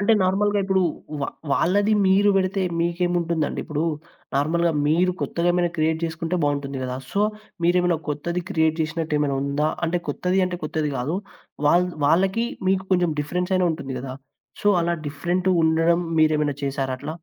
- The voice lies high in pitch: No, medium, 170 Hz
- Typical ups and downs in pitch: Yes, average, 3.2 semitones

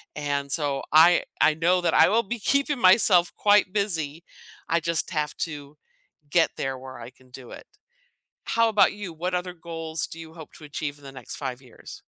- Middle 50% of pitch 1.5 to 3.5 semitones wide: No, average, 4.2 semitones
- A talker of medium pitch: Yes, medium, 165 Hz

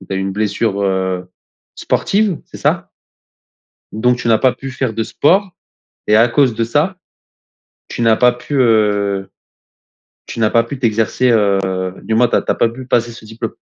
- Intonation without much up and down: No, average, 3.2 semitones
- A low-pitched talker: Yes, low, 115 Hz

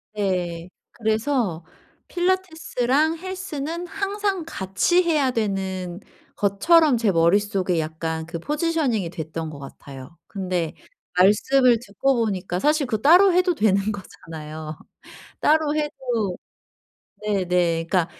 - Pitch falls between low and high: No, high, 210 Hz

